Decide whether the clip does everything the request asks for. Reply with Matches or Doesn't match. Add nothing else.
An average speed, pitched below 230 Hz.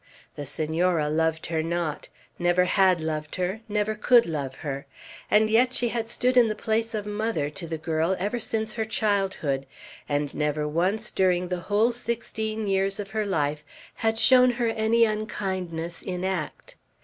Matches